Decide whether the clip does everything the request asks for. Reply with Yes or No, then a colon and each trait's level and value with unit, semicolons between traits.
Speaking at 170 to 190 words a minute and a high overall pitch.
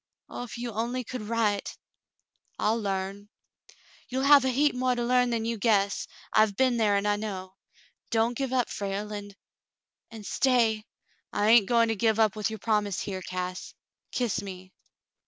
Yes: average, 180 wpm; high, 220 Hz